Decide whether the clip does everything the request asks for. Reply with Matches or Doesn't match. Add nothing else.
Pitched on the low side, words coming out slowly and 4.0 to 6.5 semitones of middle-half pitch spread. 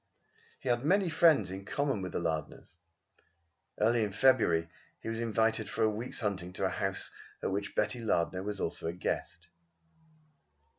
Doesn't match